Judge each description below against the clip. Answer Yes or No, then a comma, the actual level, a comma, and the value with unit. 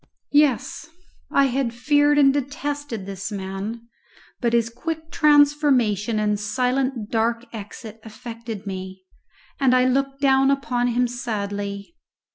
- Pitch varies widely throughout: No, average, 4.4 semitones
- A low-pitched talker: No, high, 240 Hz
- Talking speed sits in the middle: No, slow, 120 wpm